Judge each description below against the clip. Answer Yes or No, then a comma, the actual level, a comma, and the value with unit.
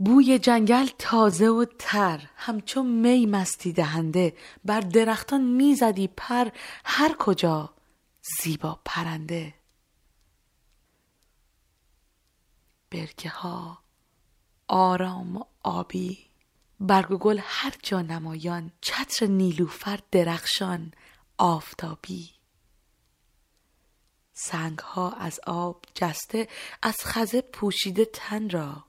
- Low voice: No, medium, 185 Hz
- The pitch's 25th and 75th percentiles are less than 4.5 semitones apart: No, average, 5.1 semitones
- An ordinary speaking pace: No, slow, 85 wpm